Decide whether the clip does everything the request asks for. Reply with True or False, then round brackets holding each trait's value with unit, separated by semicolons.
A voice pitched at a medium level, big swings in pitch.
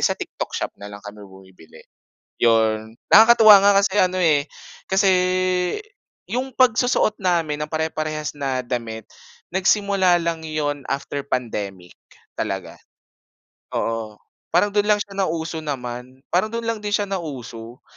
True (155 Hz; 8.5 semitones)